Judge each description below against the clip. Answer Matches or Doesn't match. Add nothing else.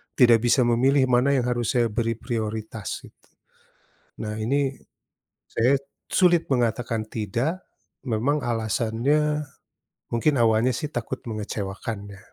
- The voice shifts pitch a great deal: Doesn't match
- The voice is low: Matches